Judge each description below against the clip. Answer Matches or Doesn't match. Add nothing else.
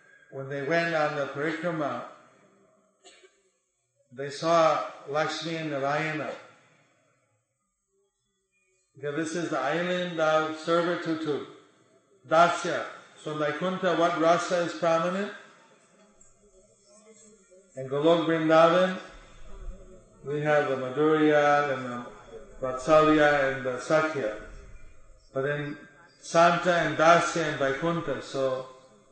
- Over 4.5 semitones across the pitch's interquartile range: Doesn't match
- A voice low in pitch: Doesn't match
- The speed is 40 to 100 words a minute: Matches